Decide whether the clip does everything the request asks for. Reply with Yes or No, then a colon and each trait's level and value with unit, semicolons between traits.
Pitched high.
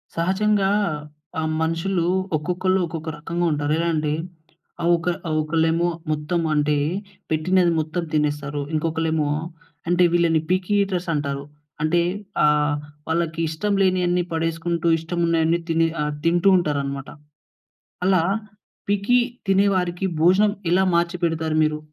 No: medium, 165 Hz